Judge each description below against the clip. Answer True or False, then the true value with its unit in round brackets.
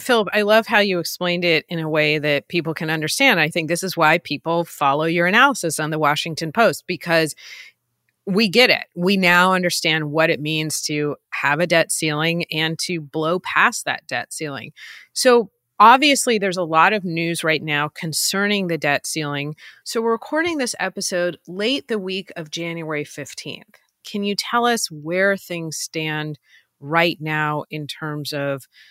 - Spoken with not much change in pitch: False (4.1 semitones)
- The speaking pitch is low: False (170 Hz)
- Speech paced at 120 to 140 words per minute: False (175 wpm)